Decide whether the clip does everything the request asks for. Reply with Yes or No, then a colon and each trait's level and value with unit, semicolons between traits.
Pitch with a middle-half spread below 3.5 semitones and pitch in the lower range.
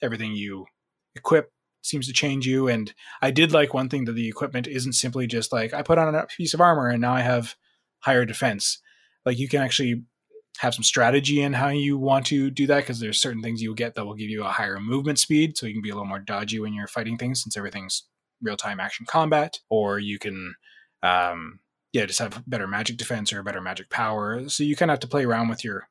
No: average, 4.7 semitones; low, 120 Hz